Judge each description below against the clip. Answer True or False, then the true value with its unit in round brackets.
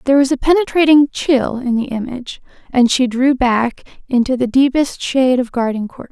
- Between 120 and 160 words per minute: False (175 wpm)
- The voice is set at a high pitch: True (260 Hz)